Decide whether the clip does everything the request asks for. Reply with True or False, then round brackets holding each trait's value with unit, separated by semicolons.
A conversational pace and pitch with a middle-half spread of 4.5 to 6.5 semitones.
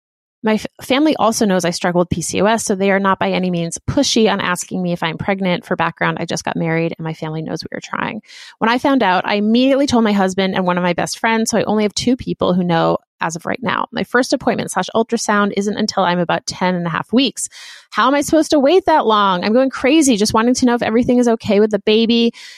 False (260 wpm; 5.0 semitones)